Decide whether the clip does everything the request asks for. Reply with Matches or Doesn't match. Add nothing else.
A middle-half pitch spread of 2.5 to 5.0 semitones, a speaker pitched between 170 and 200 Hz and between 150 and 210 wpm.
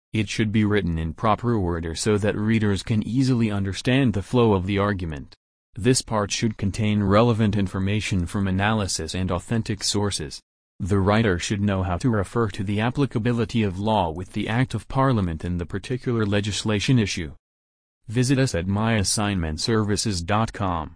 Doesn't match